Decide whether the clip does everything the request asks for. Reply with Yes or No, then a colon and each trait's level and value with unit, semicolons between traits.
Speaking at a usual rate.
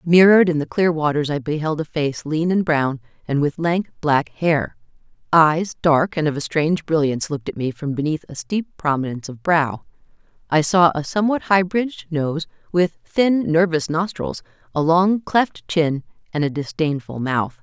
Yes: average, 180 wpm